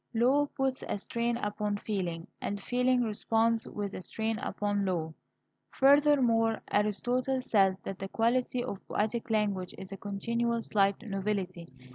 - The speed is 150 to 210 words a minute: No, average, 140 wpm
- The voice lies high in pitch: Yes, high, 215 Hz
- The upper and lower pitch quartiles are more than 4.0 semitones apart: No, average, 3.4 semitones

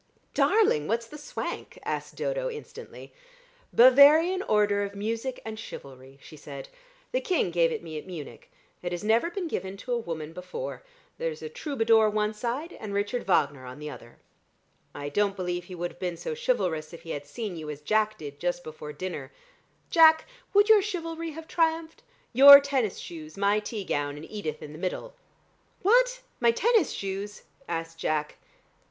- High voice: Yes, high, 210 Hz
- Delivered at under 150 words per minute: No, average, 175 wpm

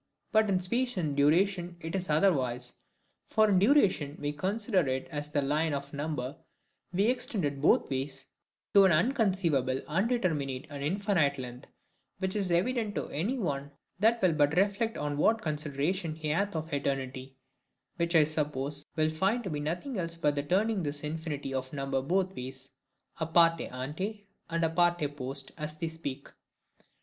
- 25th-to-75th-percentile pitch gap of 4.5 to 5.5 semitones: Yes, average, 5.1 semitones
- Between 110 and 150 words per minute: No, average, 165 wpm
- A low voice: No, medium, 160 Hz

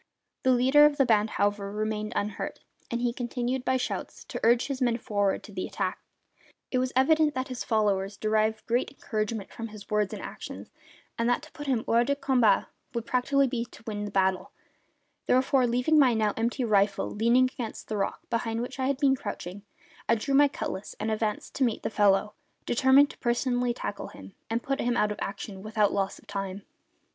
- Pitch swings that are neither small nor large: Yes, average, 3.5 semitones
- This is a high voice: Yes, high, 230 Hz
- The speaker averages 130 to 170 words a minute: No, average, 200 wpm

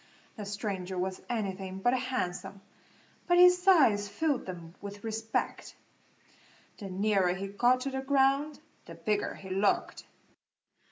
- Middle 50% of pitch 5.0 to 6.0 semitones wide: Yes, wide, 5.6 semitones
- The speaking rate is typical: No, slow, 130 wpm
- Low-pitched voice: No, high, 205 Hz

